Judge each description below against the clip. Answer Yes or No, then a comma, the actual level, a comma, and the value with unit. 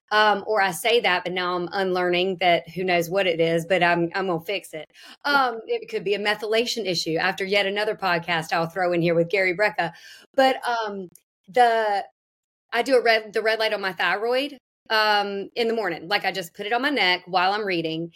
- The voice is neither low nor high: No, high, 195 Hz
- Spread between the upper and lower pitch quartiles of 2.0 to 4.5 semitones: Yes, average, 3.9 semitones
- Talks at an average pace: No, fast, 220 wpm